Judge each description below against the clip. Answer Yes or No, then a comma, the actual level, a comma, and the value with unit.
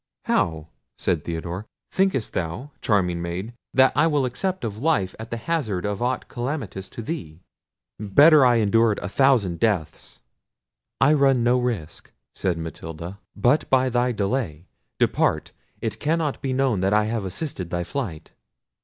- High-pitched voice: No, low, 115 Hz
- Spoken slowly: No, average, 155 wpm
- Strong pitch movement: Yes, wide, 6.4 semitones